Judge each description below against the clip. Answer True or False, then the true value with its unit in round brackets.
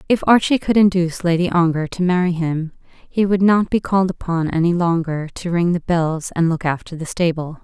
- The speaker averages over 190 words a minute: True (205 wpm)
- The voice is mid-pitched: True (175 Hz)